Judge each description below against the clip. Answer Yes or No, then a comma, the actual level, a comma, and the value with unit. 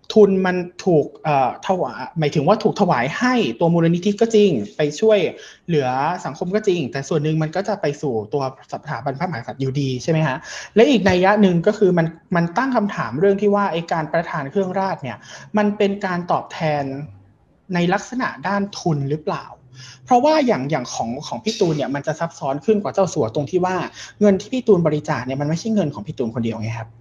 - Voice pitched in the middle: Yes, medium, 170 Hz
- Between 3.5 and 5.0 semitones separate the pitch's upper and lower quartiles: No, wide, 5.6 semitones